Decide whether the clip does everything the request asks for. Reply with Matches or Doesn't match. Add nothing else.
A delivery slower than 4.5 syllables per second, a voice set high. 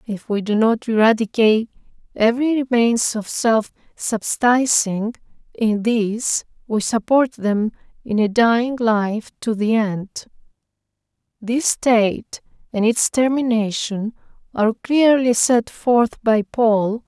Matches